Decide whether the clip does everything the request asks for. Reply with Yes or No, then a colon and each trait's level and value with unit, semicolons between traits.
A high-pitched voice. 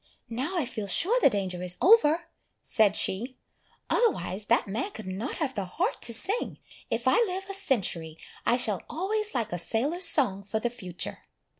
Yes: high, 240 Hz